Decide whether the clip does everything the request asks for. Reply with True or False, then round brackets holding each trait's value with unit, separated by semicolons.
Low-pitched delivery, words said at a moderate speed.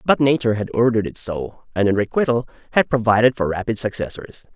True (115 Hz; 185 wpm)